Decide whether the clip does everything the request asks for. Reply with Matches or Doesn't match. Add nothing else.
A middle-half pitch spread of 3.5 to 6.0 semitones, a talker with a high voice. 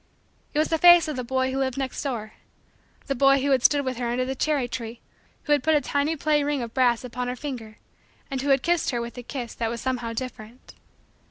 Doesn't match